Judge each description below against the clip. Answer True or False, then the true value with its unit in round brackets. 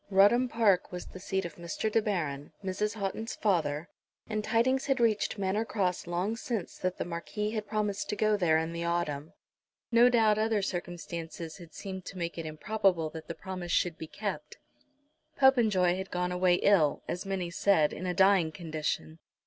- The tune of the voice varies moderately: True (3.8 semitones)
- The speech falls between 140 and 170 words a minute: False (180 wpm)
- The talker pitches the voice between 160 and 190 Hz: True (185 Hz)